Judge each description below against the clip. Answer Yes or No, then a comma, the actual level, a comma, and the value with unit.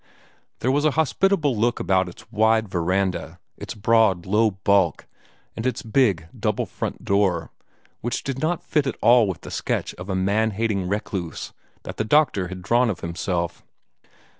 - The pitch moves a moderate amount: Yes, average, 4.3 semitones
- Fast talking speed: No, average, 165 wpm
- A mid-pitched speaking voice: No, low, 105 Hz